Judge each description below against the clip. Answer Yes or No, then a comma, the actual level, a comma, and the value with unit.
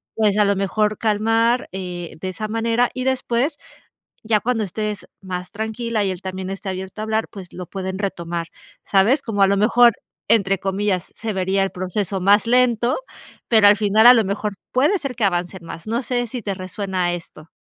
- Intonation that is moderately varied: Yes, average, 3.2 semitones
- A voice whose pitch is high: Yes, high, 205 Hz